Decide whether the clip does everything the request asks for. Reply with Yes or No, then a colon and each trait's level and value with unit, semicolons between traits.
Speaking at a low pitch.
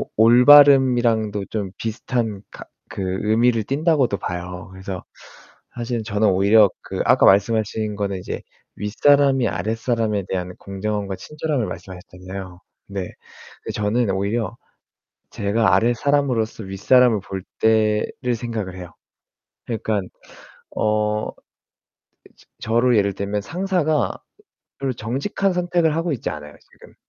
Yes: low, 110 Hz